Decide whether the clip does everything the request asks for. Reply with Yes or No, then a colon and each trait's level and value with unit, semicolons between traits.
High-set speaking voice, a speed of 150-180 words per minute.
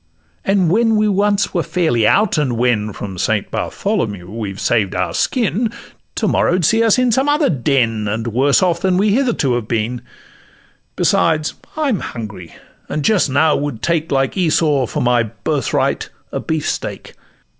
No: medium, 150 Hz; average, 170 wpm